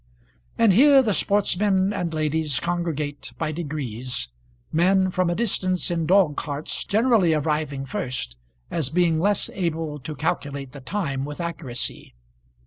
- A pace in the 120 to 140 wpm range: Yes, slow, 135 wpm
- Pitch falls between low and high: Yes, medium, 160 Hz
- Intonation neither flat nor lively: Yes, average, 4.5 semitones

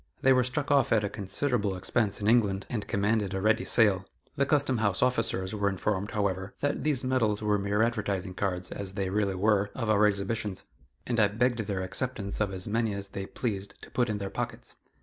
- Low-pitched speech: Yes, low, 105 Hz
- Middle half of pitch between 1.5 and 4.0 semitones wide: Yes, average, 3.2 semitones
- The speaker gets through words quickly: Yes, fast, 210 wpm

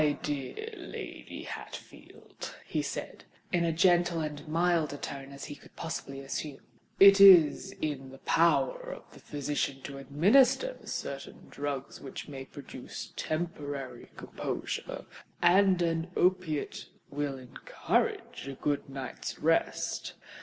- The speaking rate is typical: No, slow, 130 wpm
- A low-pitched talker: No, medium, 150 Hz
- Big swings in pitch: No, average, 4.1 semitones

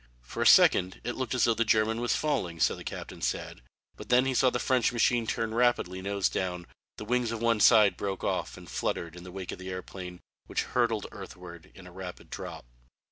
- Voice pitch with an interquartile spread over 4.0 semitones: Yes, average, 4.6 semitones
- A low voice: Yes, low, 105 Hz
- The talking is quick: Yes, fast, 220 wpm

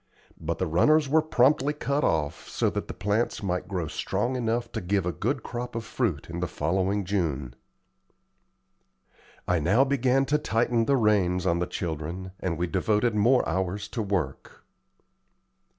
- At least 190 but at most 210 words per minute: No, average, 165 wpm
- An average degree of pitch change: No, wide, 5.7 semitones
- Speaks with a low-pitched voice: Yes, low, 100 Hz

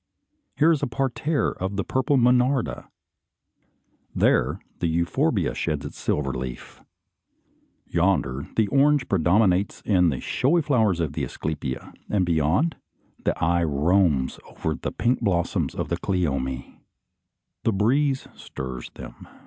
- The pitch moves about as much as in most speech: No, wide, 8.7 semitones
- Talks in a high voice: No, very low, 90 Hz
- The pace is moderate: No, slow, 130 wpm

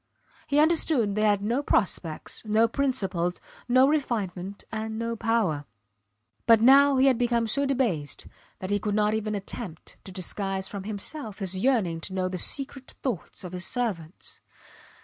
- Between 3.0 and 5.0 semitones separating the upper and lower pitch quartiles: Yes, average, 4.7 semitones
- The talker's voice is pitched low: No, high, 215 Hz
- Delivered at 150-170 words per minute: Yes, average, 160 wpm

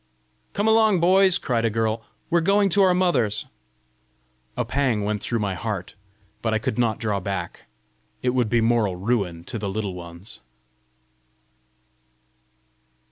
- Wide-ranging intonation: Yes, wide, 8.3 semitones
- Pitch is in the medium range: No, low, 115 Hz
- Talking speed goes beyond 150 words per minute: No, average, 145 wpm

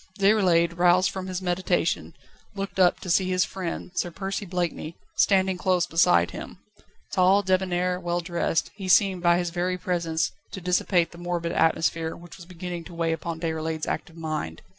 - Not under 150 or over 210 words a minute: Yes, average, 170 wpm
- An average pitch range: No, narrow, 1.8 semitones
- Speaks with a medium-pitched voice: Yes, medium, 175 Hz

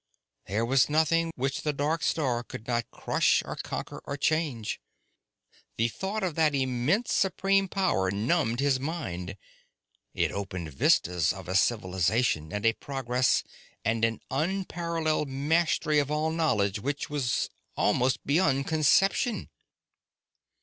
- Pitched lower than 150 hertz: Yes, low, 135 Hz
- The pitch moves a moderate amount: No, wide, 6.0 semitones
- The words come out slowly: Yes, slow, 130 wpm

